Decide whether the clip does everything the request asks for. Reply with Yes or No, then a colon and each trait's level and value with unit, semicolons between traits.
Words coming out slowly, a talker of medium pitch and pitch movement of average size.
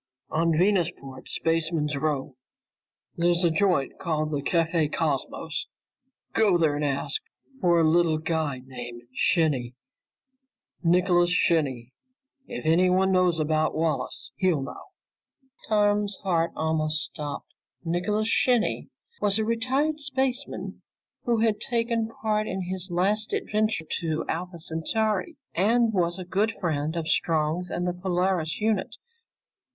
Yes: slow, 125 wpm; medium, 175 Hz; average, 4.6 semitones